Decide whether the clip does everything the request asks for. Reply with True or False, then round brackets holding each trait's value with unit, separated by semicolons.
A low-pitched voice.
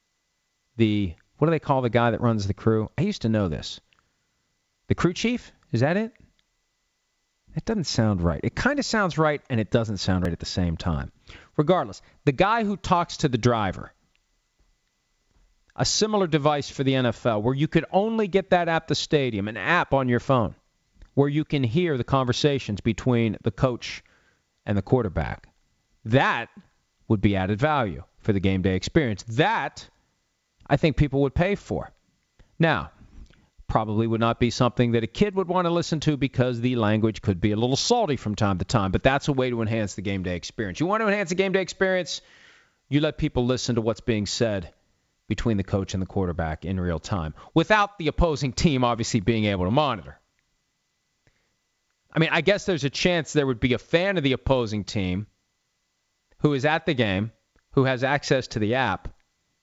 True (125 Hz)